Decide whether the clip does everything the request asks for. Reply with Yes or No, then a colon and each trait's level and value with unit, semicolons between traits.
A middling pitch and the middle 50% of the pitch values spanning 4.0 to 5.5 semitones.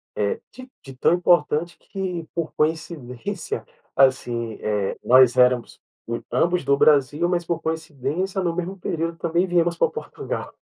Yes: medium, 165 Hz; average, 4.8 semitones